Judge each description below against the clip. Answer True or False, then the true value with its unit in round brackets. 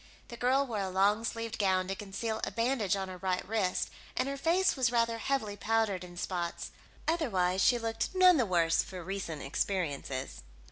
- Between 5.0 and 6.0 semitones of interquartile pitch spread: False (4.3 semitones)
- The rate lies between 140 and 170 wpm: False (185 wpm)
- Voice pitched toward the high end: True (205 Hz)